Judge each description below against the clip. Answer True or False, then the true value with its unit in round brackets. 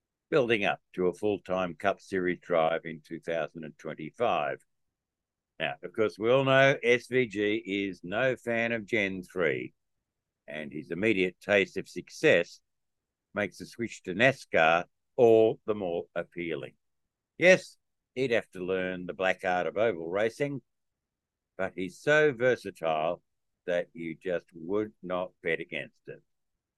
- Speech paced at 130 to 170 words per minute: True (140 wpm)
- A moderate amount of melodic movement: True (4.7 semitones)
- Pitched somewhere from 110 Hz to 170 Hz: False (95 Hz)